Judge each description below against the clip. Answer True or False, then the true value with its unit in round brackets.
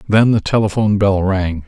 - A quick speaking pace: False (180 wpm)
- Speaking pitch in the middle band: False (100 Hz)